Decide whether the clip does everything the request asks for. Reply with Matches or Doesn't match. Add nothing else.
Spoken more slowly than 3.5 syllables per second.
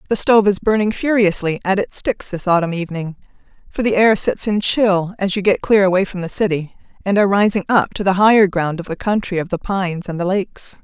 Doesn't match